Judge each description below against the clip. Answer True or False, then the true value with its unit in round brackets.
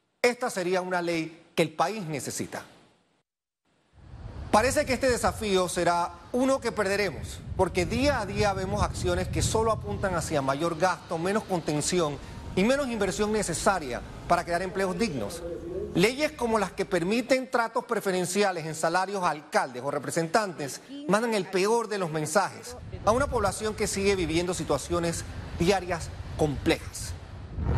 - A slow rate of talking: False (145 wpm)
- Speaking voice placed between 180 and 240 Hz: True (185 Hz)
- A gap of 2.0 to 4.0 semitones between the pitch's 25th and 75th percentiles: False (4.4 semitones)